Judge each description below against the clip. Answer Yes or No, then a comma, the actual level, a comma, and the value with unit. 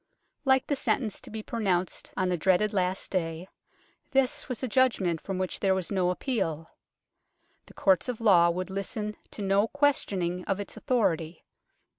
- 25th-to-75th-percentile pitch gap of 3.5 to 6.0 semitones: Yes, average, 4.0 semitones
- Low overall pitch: No, high, 195 Hz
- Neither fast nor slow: Yes, average, 165 wpm